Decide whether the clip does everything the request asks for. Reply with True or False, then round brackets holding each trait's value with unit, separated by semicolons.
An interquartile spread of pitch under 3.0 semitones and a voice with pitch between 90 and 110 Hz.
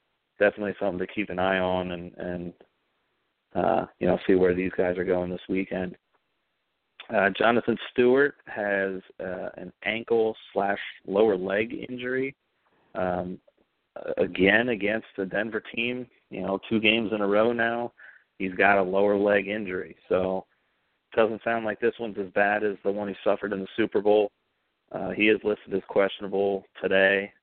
True (2.5 semitones; 100 Hz)